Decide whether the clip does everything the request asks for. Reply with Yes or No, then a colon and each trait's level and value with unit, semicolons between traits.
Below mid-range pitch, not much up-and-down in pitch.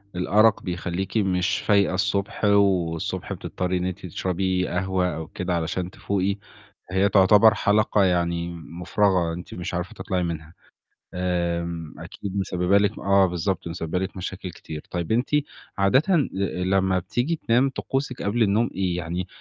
Yes: very low, 95 Hz; narrow, 2.3 semitones